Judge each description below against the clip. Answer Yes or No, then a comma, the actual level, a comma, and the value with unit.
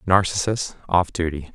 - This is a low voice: Yes, very low, 90 Hz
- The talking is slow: Yes, slow, 115 wpm